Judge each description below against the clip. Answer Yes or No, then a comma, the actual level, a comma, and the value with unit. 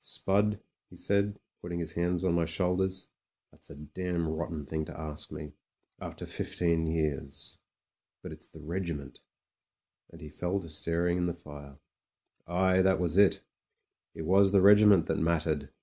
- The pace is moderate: Yes, average, 165 wpm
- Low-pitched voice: Yes, very low, 85 Hz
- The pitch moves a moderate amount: Yes, average, 3.0 semitones